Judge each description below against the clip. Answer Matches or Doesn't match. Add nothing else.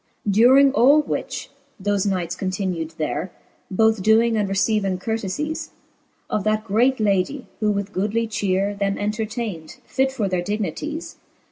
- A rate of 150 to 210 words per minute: Doesn't match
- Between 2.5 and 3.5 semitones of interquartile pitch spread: Matches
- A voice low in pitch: Doesn't match